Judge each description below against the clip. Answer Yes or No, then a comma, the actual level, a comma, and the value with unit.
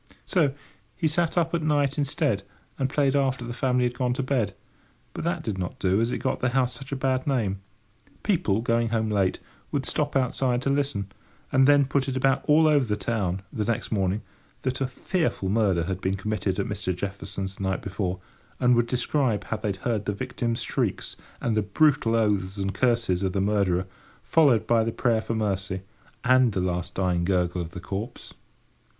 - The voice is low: Yes, low, 115 Hz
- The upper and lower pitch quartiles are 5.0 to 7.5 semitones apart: Yes, average, 5.3 semitones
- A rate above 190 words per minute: Yes, average, 200 wpm